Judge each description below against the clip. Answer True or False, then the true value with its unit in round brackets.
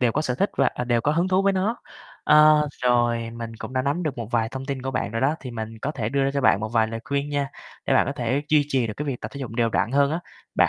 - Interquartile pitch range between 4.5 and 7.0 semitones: False (3.9 semitones)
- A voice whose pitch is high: False (130 Hz)